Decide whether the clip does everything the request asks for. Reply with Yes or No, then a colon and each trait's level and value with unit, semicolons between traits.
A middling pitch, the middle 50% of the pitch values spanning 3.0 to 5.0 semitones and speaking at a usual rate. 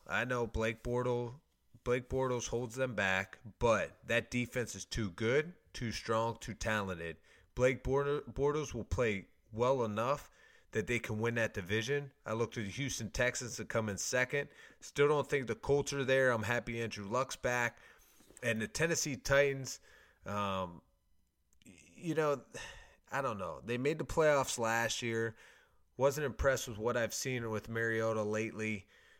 No: low, 120 Hz; average, 3.4 semitones; average, 160 wpm